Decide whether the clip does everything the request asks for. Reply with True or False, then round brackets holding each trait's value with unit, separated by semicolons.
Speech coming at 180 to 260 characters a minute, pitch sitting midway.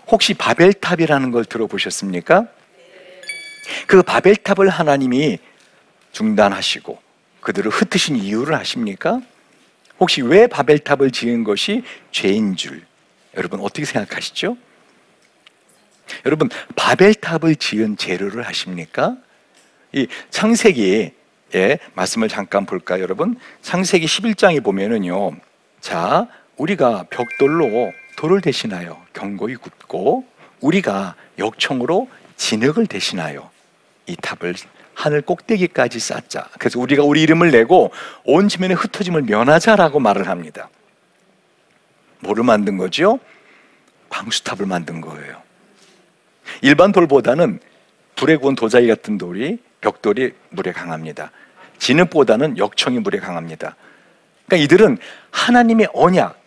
False (270 characters per minute; 160 Hz)